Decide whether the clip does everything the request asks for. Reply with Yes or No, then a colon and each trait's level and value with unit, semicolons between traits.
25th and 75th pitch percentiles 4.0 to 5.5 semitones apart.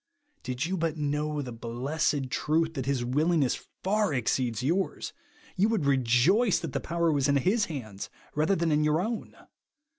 Yes: average, 4.6 semitones